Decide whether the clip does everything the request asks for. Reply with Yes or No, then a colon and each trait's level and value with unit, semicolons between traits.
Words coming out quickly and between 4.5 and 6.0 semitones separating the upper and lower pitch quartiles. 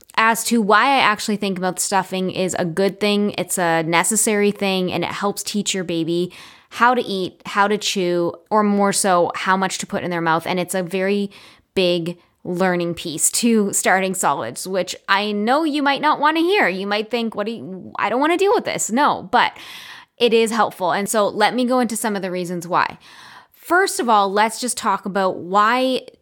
No: fast, 215 wpm; average, 3.7 semitones